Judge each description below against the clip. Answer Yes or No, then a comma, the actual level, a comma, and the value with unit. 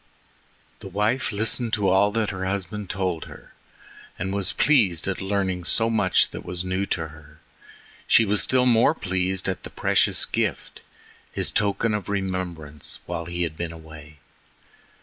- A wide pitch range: No, average, 3.0 semitones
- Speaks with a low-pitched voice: Yes, very low, 95 Hz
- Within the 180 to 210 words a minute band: No, average, 150 wpm